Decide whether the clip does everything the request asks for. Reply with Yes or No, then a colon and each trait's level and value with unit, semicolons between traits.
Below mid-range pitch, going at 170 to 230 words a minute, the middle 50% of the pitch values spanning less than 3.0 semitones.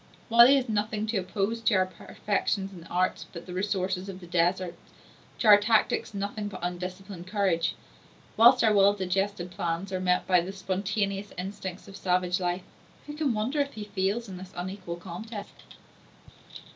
No: high, 195 Hz; average, 180 wpm; narrow, 2.4 semitones